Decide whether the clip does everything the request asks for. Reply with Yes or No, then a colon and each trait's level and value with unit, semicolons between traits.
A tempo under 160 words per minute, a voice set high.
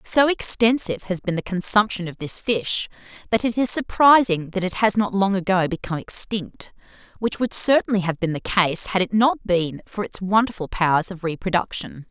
No: average, 190 wpm; high, 195 Hz